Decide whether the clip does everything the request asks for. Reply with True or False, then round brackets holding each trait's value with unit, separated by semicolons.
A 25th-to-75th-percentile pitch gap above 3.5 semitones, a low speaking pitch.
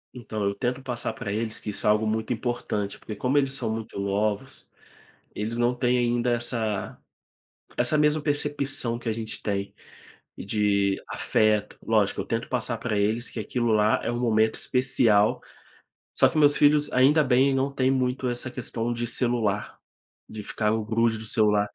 False (2.9 semitones; 115 Hz)